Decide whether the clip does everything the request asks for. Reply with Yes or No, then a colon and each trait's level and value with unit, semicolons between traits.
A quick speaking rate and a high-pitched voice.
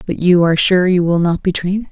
No: fast, 280 wpm; medium, 180 Hz